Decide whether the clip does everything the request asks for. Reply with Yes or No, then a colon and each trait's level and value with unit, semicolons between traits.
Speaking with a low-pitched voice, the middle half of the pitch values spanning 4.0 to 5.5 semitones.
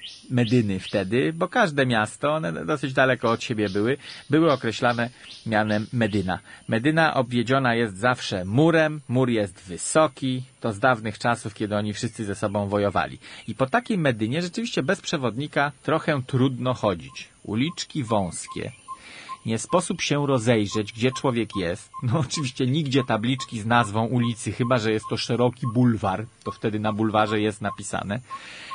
Yes: low, 120 Hz; average, 4.3 semitones